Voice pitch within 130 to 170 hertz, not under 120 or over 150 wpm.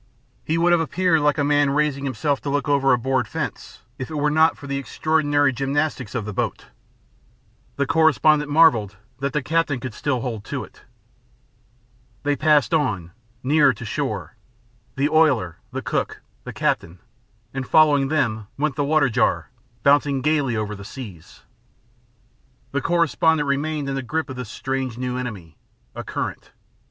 No: medium, 140 Hz; average, 165 wpm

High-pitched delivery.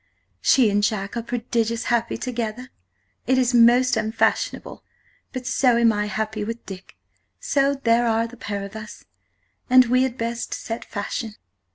Yes: high, 230 Hz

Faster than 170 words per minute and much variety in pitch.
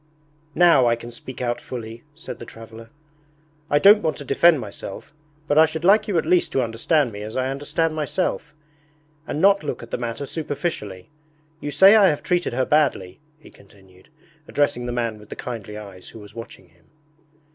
Yes: average, 190 wpm; wide, 5.9 semitones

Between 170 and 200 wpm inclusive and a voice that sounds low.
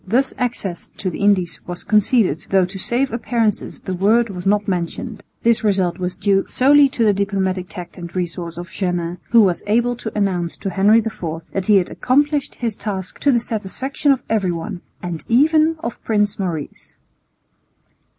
No: average, 175 wpm; high, 200 Hz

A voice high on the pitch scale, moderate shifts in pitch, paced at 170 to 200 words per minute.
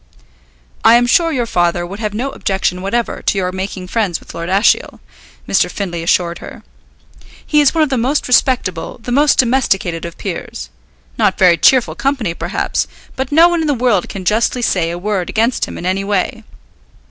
No: high, 210 Hz; wide, 5.7 semitones; average, 190 wpm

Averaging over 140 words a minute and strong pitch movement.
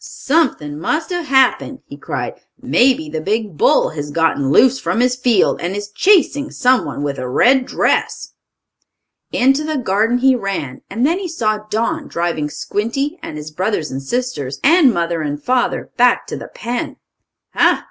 Yes: average, 170 wpm; wide, 8.7 semitones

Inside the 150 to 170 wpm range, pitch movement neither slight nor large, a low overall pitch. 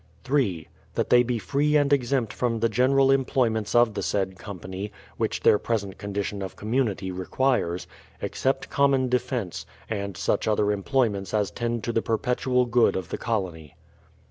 Yes: average, 165 wpm; average, 4.1 semitones; low, 115 Hz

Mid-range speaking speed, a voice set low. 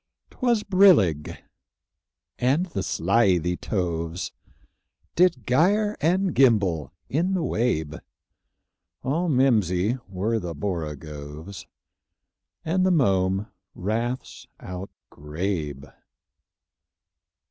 No: slow, 80 wpm; low, 100 Hz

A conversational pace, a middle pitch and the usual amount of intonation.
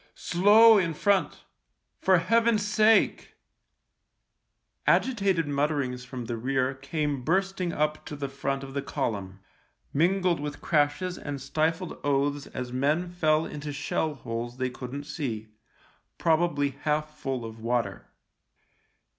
No: slow, 130 wpm; medium, 145 Hz; average, 4.4 semitones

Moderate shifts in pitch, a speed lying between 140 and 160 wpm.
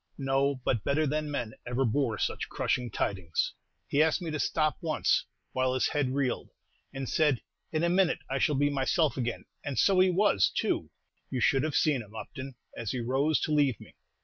No: average, 3.3 semitones; average, 200 wpm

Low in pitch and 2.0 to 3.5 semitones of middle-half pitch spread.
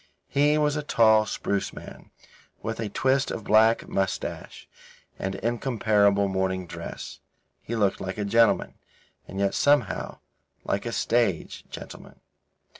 Yes: low, 110 Hz; average, 3.1 semitones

